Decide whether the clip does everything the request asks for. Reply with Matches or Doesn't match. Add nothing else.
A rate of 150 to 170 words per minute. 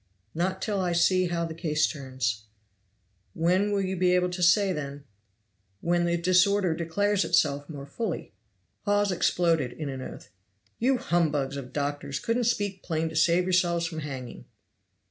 Matches